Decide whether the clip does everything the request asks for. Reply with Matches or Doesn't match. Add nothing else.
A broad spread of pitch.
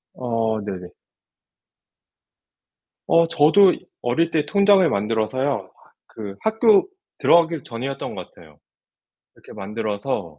Matches